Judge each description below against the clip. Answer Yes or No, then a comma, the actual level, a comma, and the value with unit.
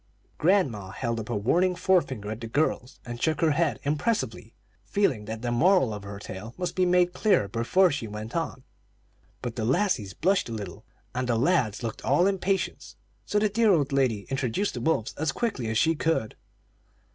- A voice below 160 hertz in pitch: Yes, low, 135 Hz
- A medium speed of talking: Yes, average, 190 wpm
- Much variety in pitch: Yes, wide, 8.1 semitones